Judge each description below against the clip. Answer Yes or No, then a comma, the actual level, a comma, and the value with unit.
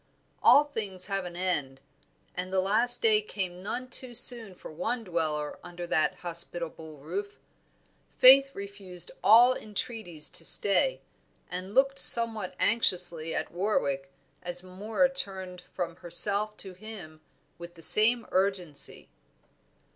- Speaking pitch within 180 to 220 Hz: Yes, high, 190 Hz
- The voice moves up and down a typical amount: Yes, average, 4.2 semitones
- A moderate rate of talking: No, slow, 130 wpm